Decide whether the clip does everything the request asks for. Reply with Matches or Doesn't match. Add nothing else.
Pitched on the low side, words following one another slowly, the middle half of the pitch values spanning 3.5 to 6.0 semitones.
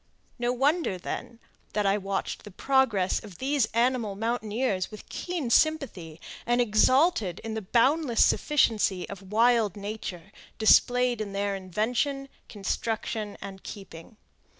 Doesn't match